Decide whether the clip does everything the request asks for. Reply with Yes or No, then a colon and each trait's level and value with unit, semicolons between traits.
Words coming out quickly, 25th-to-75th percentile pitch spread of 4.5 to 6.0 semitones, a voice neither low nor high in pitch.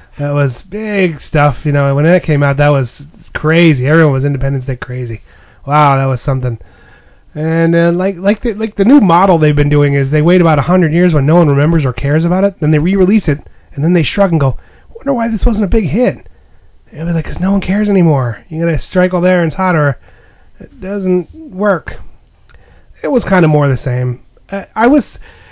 Yes: fast, 220 wpm; average, 5.3 semitones; medium, 155 Hz